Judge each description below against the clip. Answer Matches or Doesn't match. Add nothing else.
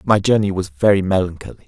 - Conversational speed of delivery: Matches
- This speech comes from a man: Matches